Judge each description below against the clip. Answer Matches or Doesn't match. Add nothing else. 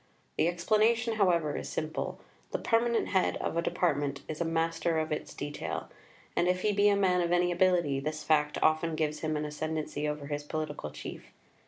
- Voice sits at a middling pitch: Matches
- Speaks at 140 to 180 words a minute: Doesn't match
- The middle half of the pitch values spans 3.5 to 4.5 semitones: Doesn't match